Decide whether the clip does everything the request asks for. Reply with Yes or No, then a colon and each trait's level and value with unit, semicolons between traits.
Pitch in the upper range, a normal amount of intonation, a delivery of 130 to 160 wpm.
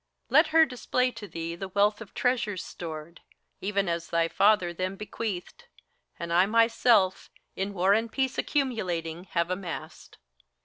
Yes: high, 195 Hz; average, 4.8 semitones; average, 145 wpm